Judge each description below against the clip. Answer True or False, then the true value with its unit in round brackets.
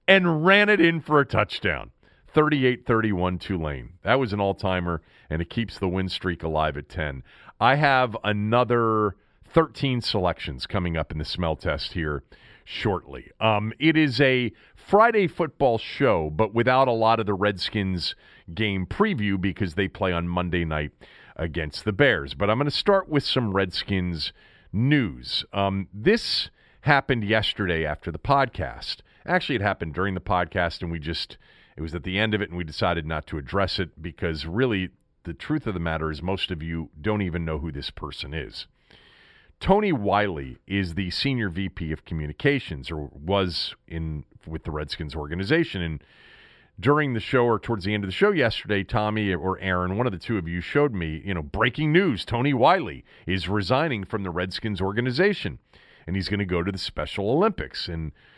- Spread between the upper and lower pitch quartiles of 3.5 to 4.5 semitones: False (5.5 semitones)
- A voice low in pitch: True (95 Hz)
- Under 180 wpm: False (185 wpm)